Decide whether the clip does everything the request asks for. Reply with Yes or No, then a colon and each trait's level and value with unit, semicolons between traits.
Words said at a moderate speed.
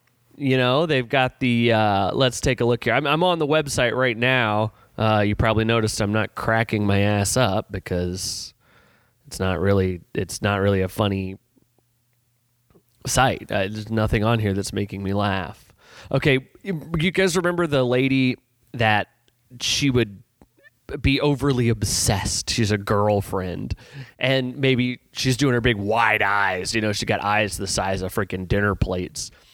Yes: average, 165 wpm